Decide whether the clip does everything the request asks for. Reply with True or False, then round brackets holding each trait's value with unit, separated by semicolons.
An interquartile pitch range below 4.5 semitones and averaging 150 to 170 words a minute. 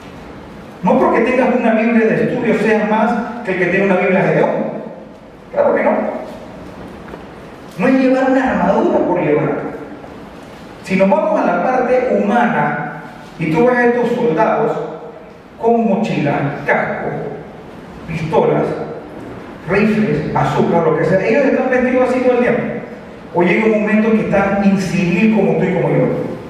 True (4.1 semitones; 155 wpm)